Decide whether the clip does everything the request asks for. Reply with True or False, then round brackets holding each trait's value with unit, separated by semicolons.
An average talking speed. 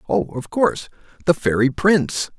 True (150 wpm)